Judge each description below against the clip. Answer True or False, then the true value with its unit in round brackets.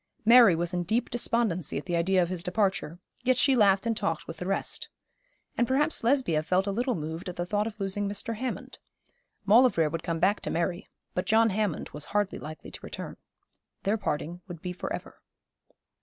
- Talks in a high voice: True (195 Hz)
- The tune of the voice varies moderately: True (4.6 semitones)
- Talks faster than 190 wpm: True (200 wpm)